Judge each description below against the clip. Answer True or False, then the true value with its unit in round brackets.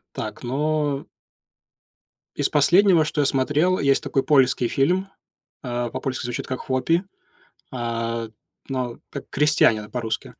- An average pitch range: True (3.7 semitones)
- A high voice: False (135 Hz)